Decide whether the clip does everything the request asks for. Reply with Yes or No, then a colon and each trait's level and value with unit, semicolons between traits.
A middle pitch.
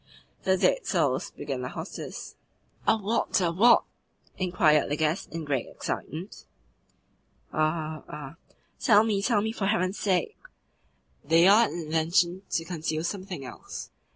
Yes: medium, 175 Hz